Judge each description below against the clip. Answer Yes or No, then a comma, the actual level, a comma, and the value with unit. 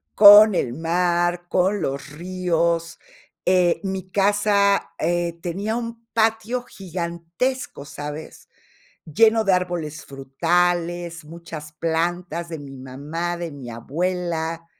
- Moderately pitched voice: Yes, medium, 175 Hz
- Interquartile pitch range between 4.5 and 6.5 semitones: No, average, 2.7 semitones